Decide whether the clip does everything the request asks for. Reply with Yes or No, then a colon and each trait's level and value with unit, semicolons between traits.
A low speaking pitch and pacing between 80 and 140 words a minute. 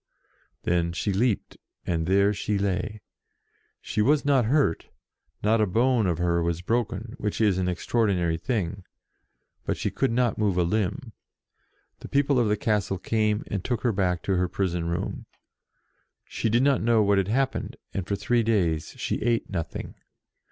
No: low, 105 Hz; average, 170 wpm